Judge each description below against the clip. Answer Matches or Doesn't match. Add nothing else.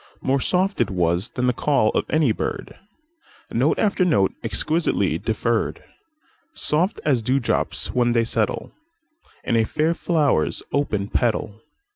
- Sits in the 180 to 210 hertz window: Doesn't match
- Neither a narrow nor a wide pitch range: Doesn't match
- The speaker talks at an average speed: Doesn't match